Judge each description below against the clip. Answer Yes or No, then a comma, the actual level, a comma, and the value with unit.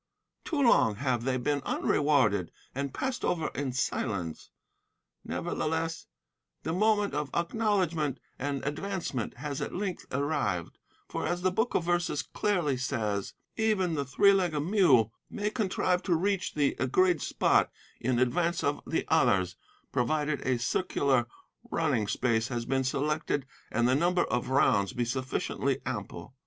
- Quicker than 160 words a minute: No, average, 145 wpm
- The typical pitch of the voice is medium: Yes, medium, 145 Hz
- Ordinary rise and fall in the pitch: No, wide, 5.9 semitones